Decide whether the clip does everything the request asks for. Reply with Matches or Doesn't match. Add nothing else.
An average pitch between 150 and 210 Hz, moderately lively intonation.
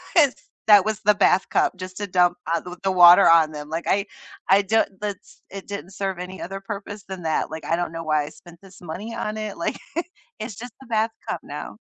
Matches